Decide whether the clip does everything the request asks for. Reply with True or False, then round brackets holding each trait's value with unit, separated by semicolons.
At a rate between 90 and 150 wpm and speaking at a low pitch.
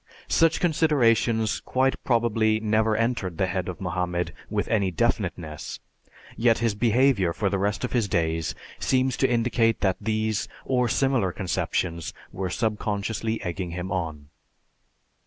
True (140 wpm; 110 Hz)